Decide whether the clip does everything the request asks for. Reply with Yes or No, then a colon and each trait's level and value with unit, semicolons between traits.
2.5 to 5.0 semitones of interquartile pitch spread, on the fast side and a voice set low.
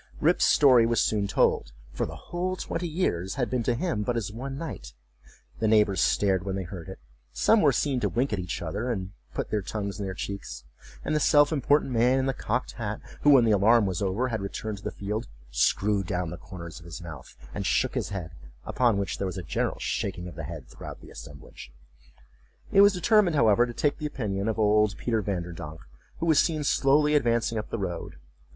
No: wide, 5.6 semitones; fast, 215 wpm; low, 105 Hz